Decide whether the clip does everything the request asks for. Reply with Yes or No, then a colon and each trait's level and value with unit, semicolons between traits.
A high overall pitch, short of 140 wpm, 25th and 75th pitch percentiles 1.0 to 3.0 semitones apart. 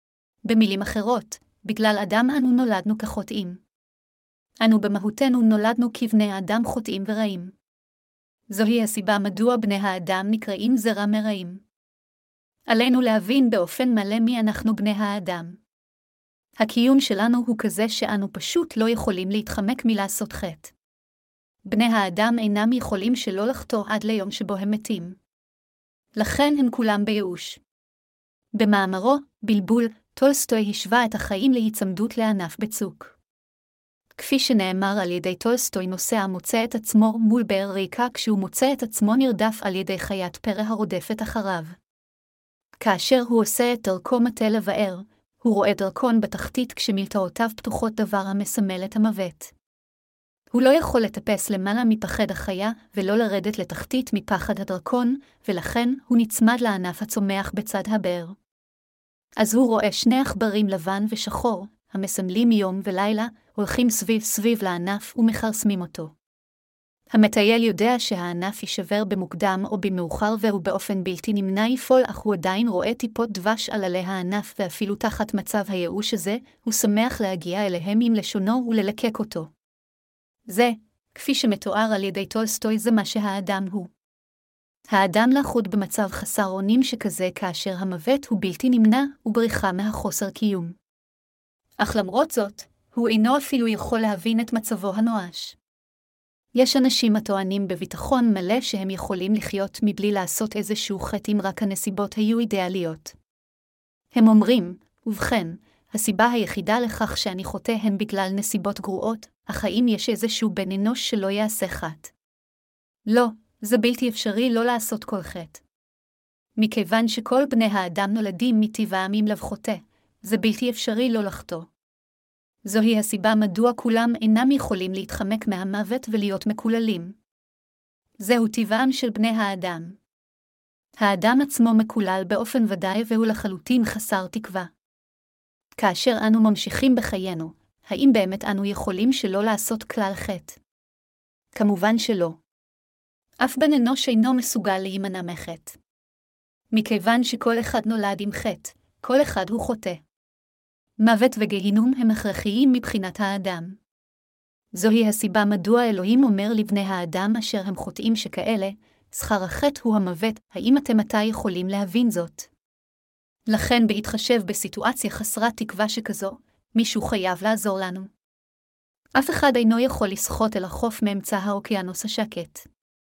Yes: high, 215 Hz; average, 130 wpm; average, 2.7 semitones